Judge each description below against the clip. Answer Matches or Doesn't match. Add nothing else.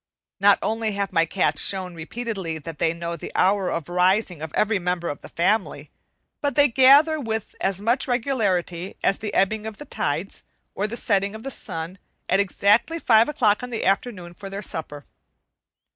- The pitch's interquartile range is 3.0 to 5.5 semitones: Matches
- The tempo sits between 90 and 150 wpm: Doesn't match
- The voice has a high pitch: Matches